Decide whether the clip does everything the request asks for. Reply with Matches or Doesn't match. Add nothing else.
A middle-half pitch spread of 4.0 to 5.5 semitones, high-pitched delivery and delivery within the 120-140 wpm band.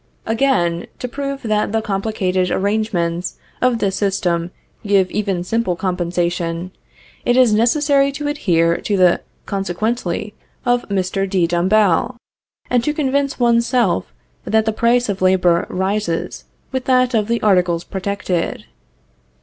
Matches